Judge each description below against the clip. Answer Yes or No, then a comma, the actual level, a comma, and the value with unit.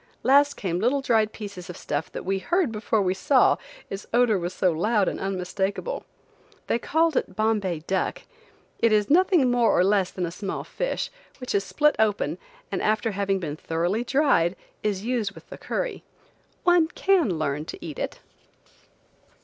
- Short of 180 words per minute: Yes, average, 170 wpm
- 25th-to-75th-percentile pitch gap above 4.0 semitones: Yes, average, 5.3 semitones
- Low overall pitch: No, high, 210 Hz